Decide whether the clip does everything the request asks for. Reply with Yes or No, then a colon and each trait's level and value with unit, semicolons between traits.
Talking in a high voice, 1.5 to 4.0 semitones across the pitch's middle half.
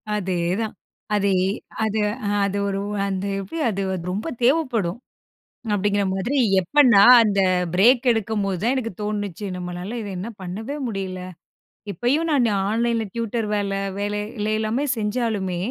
Yes: high, 210 Hz; average, 3.0 semitones